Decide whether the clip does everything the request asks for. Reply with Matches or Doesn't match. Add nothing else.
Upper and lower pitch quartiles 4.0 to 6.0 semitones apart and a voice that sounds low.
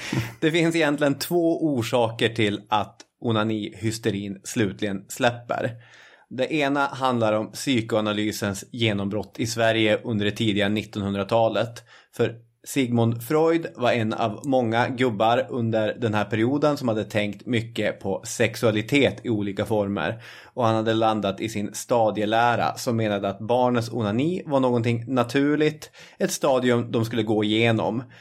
Doesn't match